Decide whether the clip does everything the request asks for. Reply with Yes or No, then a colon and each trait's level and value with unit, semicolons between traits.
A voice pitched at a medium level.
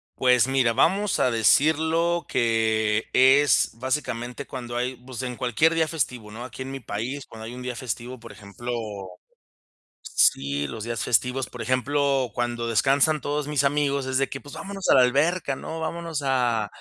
No: low, 130 Hz